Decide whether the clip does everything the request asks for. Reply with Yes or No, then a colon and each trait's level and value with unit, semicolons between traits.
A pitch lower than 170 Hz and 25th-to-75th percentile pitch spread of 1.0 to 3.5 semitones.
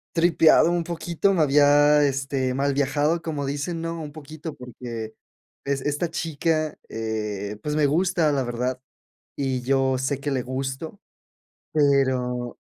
Yes: medium, 140 Hz; average, 3.2 semitones